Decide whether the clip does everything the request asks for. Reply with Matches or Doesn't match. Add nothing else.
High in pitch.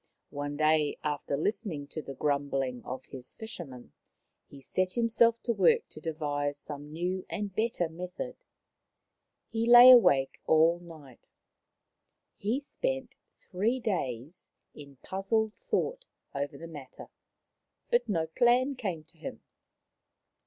Doesn't match